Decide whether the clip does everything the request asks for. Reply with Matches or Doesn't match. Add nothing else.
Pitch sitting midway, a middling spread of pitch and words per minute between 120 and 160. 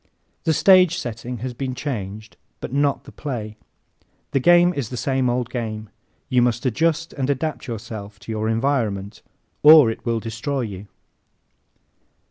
Doesn't match